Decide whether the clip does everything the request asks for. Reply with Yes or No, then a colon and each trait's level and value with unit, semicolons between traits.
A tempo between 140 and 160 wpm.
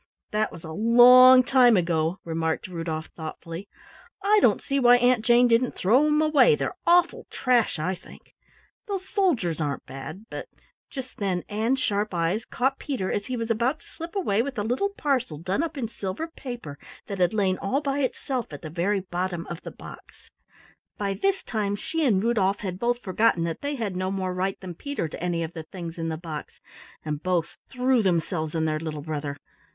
No: average, 200 wpm